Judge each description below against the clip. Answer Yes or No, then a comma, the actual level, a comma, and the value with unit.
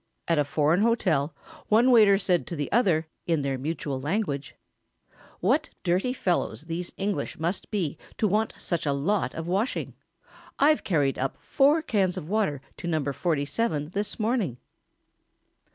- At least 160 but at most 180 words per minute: No, average, 150 wpm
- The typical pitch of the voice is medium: Yes, medium, 175 Hz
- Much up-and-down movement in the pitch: Yes, wide, 6.0 semitones